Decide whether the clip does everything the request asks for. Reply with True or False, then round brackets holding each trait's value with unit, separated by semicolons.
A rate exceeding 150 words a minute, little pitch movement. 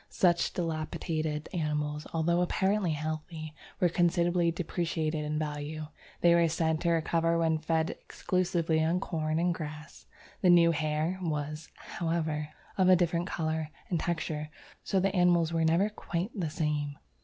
False (145 wpm; 2.0 semitones)